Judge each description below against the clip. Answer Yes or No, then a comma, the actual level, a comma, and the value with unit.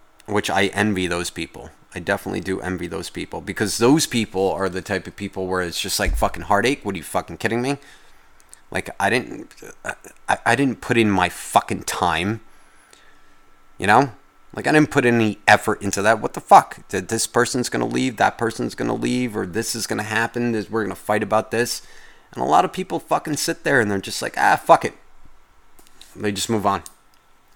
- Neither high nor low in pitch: No, low, 105 Hz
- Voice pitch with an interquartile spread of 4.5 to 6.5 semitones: No, average, 3.3 semitones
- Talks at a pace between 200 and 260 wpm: Yes, fast, 205 wpm